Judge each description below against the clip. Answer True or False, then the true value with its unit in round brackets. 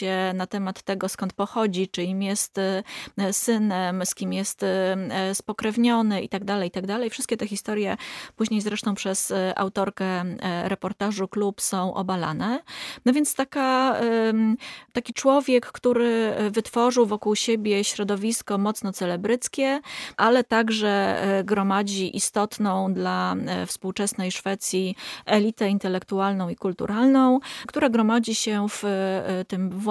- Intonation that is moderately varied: True (3.2 semitones)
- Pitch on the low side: False (205 Hz)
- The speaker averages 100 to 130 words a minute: True (120 wpm)